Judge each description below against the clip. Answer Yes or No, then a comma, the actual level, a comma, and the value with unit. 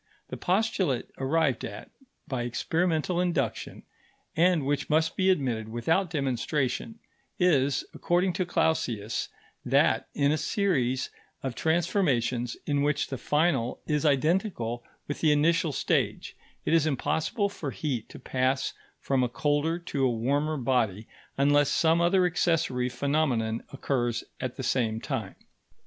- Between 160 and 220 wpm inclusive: No, slow, 135 wpm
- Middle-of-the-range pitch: Yes, medium, 145 Hz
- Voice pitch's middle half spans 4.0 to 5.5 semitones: Yes, average, 4.7 semitones